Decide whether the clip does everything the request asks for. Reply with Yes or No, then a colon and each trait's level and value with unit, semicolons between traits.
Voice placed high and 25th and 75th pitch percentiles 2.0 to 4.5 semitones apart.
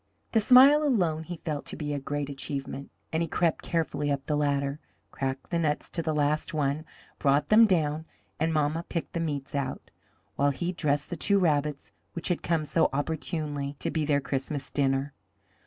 No: medium, 150 Hz; average, 2.8 semitones